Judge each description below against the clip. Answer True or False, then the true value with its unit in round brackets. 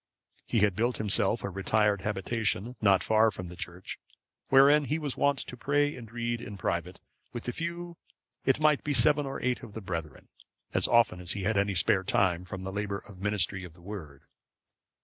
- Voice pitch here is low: True (105 Hz)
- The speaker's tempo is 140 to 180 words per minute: False (200 wpm)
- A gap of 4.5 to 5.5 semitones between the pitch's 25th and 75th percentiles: True (4.8 semitones)